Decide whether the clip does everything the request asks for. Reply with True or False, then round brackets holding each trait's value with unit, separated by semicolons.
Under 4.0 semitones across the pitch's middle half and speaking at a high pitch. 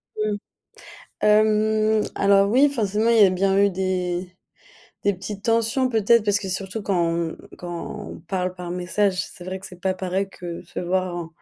True (2.8 semitones; 195 Hz)